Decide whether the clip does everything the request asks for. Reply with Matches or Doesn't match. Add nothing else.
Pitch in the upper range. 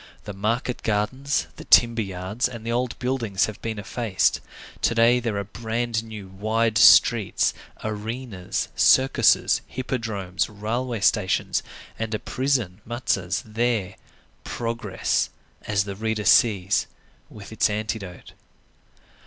Doesn't match